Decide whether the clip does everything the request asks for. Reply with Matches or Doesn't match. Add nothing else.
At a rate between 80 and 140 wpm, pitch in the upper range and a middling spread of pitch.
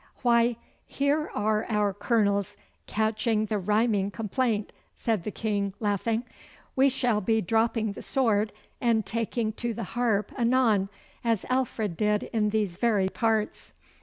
Doesn't match